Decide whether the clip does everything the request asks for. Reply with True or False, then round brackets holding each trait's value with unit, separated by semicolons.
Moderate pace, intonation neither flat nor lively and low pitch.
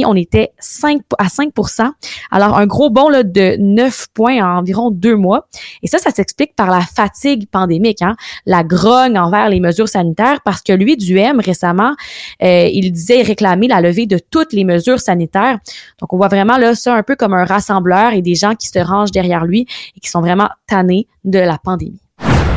False (200 wpm; 4.4 semitones; 205 Hz)